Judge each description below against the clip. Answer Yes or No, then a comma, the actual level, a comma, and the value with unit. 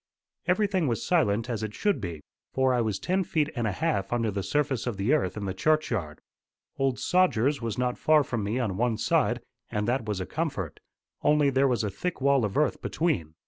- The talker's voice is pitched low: Yes, low, 125 Hz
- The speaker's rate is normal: No, fast, 220 wpm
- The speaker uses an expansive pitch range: Yes, wide, 6.2 semitones